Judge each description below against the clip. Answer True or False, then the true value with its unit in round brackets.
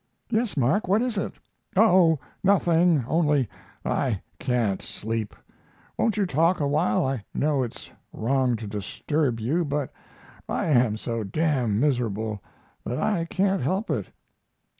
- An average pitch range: False (7.1 semitones)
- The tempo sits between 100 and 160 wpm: True (140 wpm)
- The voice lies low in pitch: False (145 Hz)